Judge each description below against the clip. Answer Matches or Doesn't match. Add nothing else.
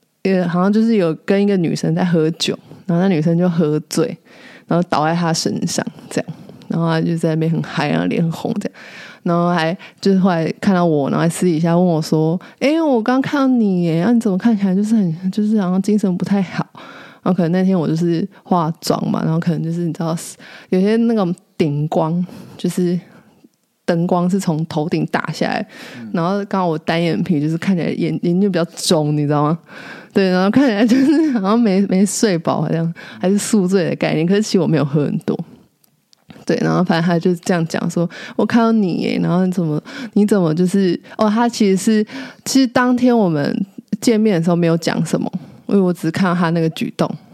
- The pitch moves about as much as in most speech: Matches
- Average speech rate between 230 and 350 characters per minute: Matches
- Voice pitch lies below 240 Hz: Matches